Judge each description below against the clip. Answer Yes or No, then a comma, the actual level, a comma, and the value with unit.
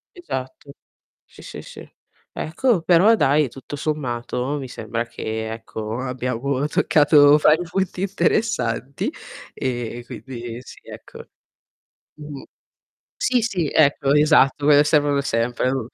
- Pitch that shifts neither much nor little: Yes, average, 4.1 semitones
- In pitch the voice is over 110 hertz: Yes, medium, 140 Hz